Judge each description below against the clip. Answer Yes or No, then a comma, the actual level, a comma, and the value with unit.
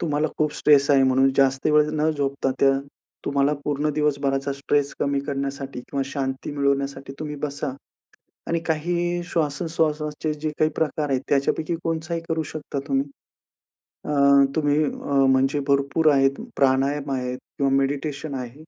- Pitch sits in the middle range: Yes, medium, 145 Hz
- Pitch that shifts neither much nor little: No, narrow, 1.9 semitones